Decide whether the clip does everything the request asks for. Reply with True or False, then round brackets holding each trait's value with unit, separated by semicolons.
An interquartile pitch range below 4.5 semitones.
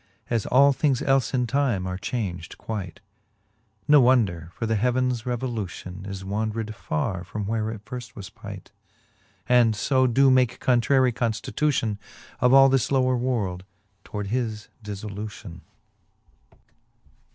True (3.9 semitones)